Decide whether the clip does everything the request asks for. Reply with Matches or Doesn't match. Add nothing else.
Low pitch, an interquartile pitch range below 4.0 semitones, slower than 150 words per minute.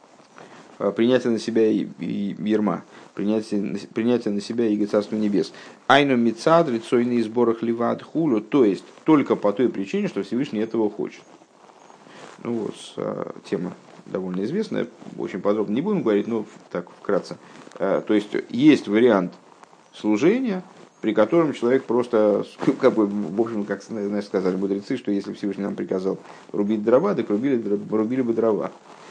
Doesn't match